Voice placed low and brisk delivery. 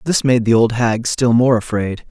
Yes: low, 120 Hz; fast, 230 wpm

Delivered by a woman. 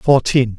No: male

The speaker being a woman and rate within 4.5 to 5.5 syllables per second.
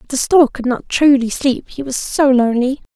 Yes: female; 5.1 syllables/s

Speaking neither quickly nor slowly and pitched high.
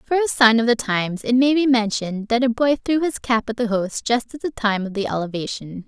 No: fast, 265 wpm; high, 235 Hz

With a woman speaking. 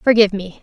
Yes: female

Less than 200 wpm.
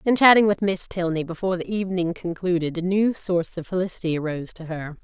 No: fast, 205 wpm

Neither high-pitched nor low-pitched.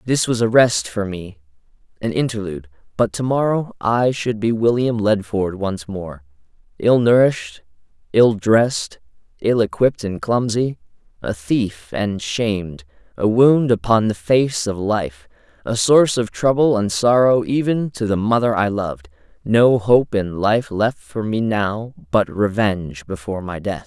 No: low, 110 Hz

